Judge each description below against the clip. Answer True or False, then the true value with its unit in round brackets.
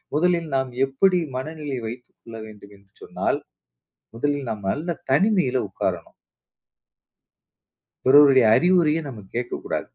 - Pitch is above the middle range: False (135 Hz)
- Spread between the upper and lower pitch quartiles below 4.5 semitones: False (5.1 semitones)